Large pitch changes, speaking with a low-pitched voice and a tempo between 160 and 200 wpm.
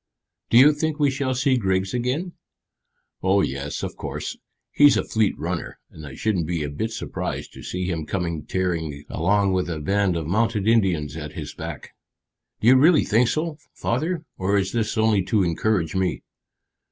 Yes: wide, 6.2 semitones; low, 100 Hz; average, 180 wpm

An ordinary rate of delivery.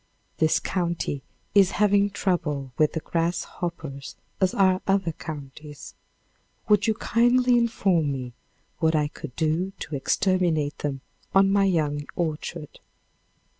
No: slow, 125 wpm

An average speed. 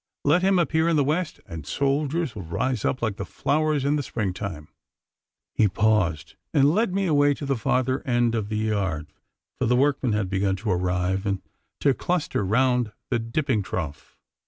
Yes: average, 185 wpm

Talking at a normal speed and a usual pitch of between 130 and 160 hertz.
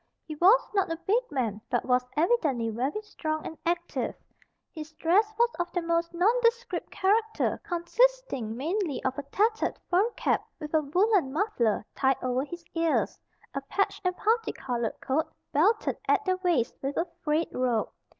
No: average, 165 wpm; very high, 335 Hz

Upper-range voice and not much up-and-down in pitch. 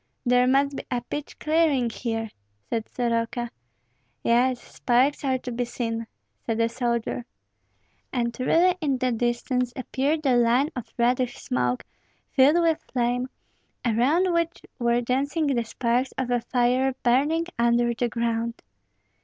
Yes: high, 245 Hz; narrow, 2.3 semitones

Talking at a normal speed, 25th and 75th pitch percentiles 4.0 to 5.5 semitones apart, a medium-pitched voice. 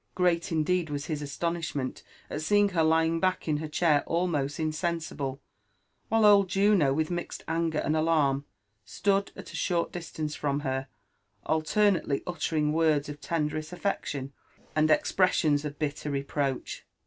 No: average, 145 wpm; average, 2.9 semitones; medium, 155 Hz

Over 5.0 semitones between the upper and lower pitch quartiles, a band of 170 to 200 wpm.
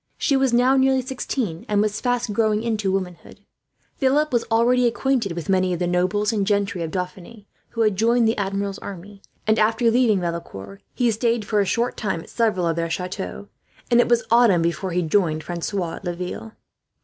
No: average, 4.5 semitones; average, 195 wpm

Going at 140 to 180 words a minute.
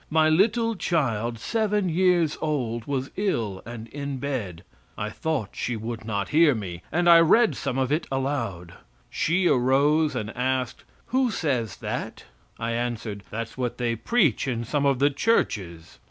Yes: average, 160 wpm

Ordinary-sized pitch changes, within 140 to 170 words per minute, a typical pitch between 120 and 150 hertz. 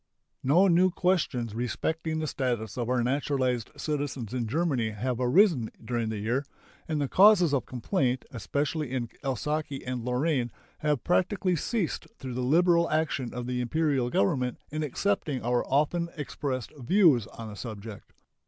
Yes: average, 4.5 semitones; average, 155 wpm; low, 135 Hz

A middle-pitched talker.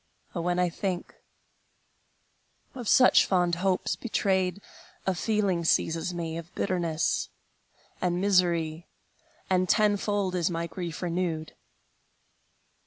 Yes: medium, 180 Hz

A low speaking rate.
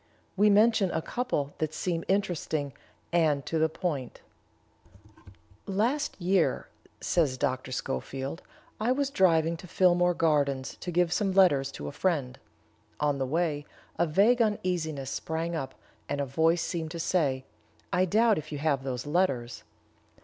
No: average, 150 wpm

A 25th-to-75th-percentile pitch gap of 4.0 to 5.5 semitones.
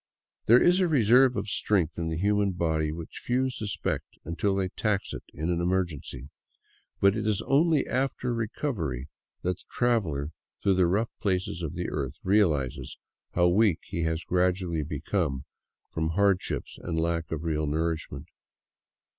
Yes: average, 4.8 semitones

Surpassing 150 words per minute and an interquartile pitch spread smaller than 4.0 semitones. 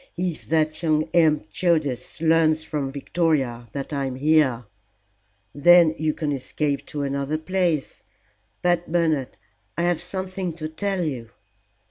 No: average, 140 wpm; average, 3.5 semitones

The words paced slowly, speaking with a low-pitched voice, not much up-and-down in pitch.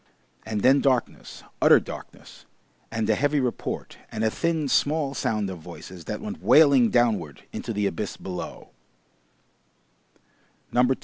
No: slow, 130 wpm; low, 120 Hz; wide, 5.4 semitones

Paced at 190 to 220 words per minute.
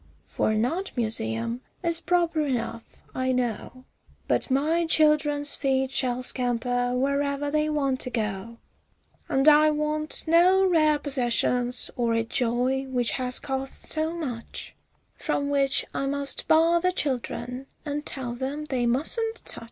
No: average, 145 wpm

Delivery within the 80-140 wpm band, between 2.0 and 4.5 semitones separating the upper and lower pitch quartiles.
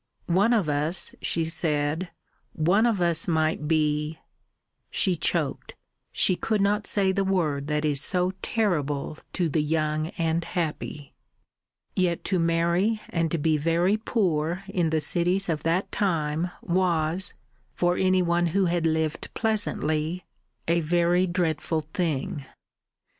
Yes: slow, 135 wpm; average, 2.9 semitones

